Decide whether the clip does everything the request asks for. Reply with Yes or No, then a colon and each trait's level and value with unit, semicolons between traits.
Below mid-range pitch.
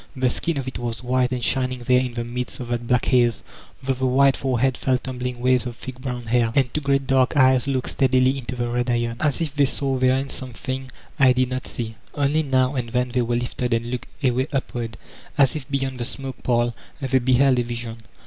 Yes: low, 125 Hz